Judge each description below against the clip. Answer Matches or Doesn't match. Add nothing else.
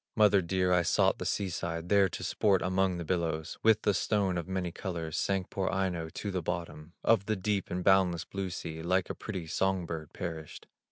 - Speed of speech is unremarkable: Doesn't match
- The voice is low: Matches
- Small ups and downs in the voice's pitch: Matches